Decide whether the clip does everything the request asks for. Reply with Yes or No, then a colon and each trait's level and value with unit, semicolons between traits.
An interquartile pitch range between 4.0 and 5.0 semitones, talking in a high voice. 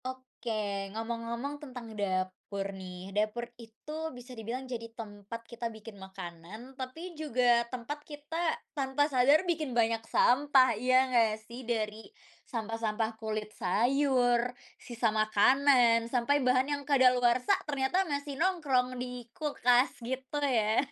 No: average, 3.2 semitones; high, 245 Hz